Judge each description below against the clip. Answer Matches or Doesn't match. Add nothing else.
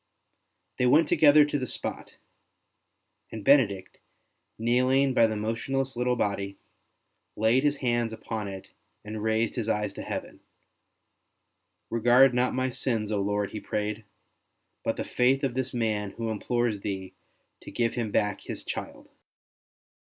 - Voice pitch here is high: Doesn't match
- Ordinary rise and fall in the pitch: Matches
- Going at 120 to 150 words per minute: Matches